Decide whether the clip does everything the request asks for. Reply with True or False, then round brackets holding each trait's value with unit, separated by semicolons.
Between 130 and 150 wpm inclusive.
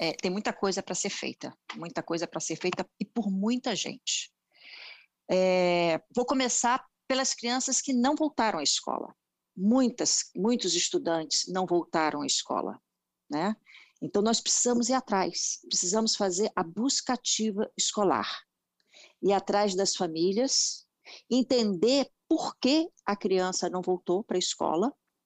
True (140 wpm)